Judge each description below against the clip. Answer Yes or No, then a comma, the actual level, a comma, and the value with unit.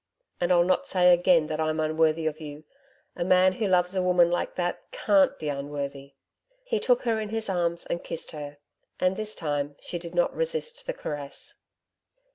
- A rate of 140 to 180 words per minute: No, average, 190 wpm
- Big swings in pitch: No, average, 3.7 semitones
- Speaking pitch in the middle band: Yes, medium, 175 Hz